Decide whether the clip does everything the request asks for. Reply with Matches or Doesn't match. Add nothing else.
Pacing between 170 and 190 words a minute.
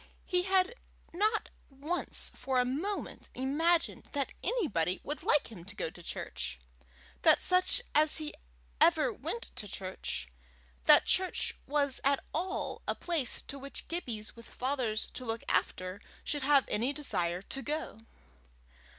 Doesn't match